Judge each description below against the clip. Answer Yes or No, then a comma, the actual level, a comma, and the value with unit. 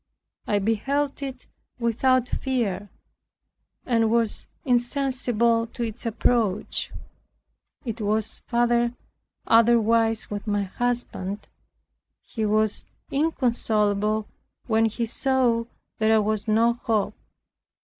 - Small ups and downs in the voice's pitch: Yes, narrow, 2.1 semitones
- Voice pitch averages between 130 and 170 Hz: No, high, 230 Hz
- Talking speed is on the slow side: Yes, slow, 95 wpm